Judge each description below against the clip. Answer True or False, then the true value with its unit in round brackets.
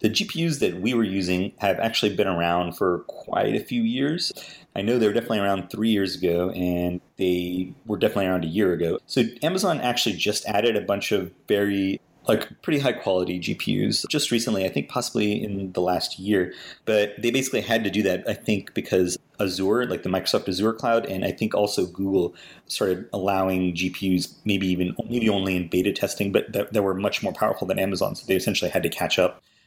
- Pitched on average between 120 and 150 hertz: False (95 Hz)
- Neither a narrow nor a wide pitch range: True (3.4 semitones)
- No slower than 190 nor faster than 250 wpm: True (205 wpm)